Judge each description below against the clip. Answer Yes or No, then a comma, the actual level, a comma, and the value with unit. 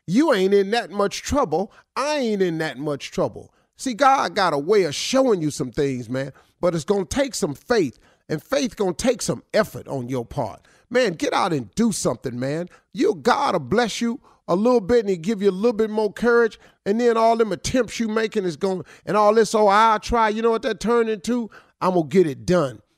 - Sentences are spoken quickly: Yes, fast, 225 wpm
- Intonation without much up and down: No, wide, 5.6 semitones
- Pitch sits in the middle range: No, high, 210 Hz